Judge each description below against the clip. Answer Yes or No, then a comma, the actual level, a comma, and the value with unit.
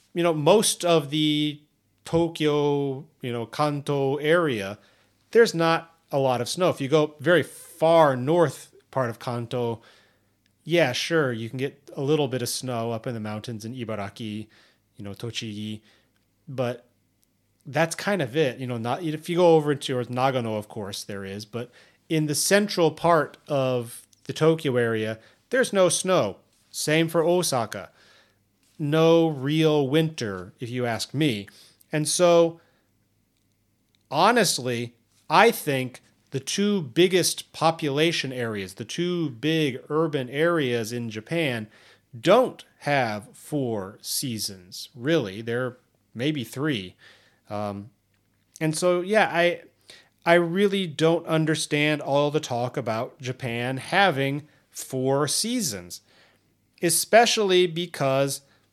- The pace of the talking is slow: Yes, slow, 130 wpm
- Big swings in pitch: Yes, wide, 6.3 semitones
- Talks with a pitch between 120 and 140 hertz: Yes, low, 135 Hz